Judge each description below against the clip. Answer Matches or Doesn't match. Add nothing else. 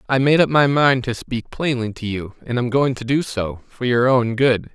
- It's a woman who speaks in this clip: Doesn't match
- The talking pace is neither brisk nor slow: Doesn't match